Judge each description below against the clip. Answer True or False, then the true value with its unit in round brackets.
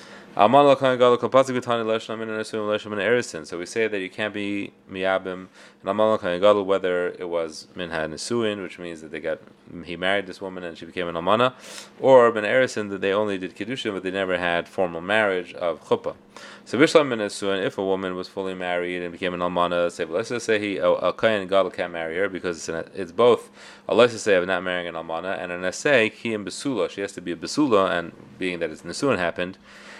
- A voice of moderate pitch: False (95 Hz)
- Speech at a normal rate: True (170 wpm)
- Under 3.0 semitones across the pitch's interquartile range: False (3.5 semitones)